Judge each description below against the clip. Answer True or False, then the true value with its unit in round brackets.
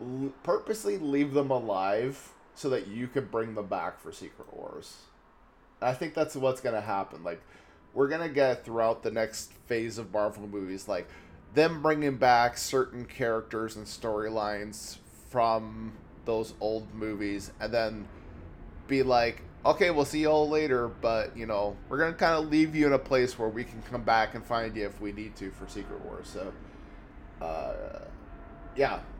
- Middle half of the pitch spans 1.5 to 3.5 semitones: False (4.2 semitones)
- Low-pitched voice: True (115 Hz)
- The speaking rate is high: False (170 wpm)